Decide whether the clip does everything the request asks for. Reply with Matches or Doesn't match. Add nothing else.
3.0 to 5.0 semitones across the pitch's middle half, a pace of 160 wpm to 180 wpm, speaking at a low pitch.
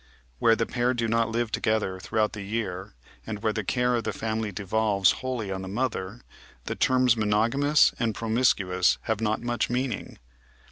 Doesn't match